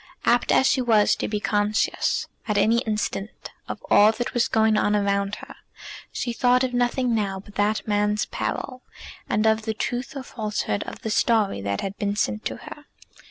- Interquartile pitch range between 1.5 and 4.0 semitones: Yes, narrow, 2.6 semitones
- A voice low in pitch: No, high, 215 Hz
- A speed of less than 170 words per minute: No, average, 190 wpm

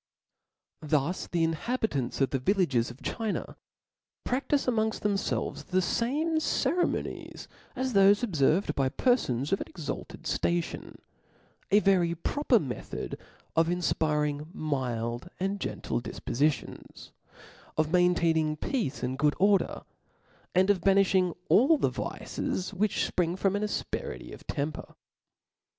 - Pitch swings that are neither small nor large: No, wide, 5.7 semitones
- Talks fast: No, slow, 135 wpm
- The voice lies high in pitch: No, medium, 180 Hz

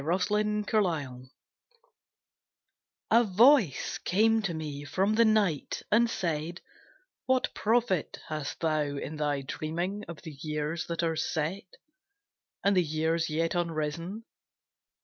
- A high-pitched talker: No, medium, 170 Hz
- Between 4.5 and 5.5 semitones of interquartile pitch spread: Yes, average, 5.2 semitones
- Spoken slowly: Yes, slow, 130 wpm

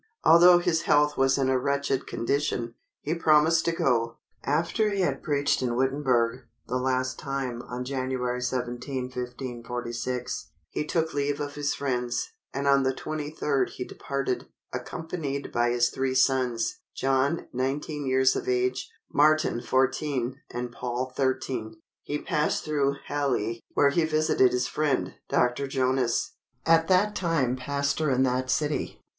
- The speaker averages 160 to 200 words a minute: No, average, 145 wpm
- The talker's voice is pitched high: No, low, 135 Hz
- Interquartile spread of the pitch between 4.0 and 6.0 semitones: No, average, 2.8 semitones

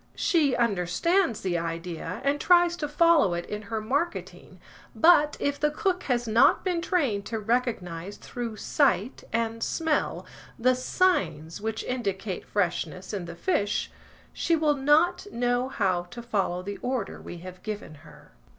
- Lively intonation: Yes, wide, 8.1 semitones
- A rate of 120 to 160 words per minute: Yes, average, 150 wpm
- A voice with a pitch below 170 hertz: No, high, 230 Hz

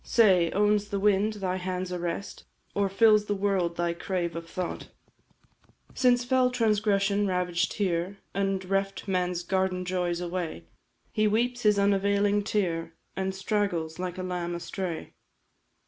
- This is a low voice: No, high, 190 Hz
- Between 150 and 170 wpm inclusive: No, average, 140 wpm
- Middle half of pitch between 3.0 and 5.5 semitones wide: No, narrow, 2.5 semitones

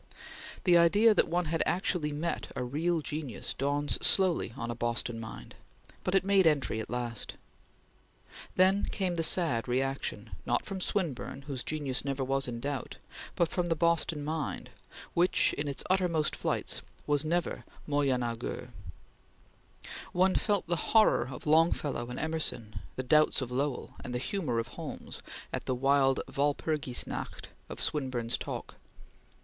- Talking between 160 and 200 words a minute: No, average, 150 wpm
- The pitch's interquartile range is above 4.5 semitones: Yes, average, 4.9 semitones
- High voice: No, medium, 145 Hz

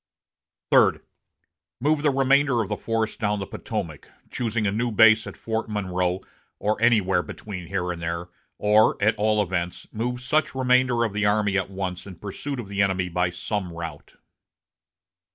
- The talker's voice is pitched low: Yes, low, 105 Hz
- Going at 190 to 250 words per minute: No, average, 170 wpm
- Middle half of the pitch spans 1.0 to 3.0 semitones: No, average, 3.9 semitones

